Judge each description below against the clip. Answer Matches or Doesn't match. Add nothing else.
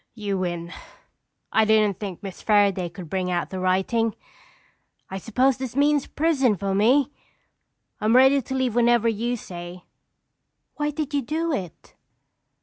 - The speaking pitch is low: Doesn't match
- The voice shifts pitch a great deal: Matches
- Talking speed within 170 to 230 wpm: Doesn't match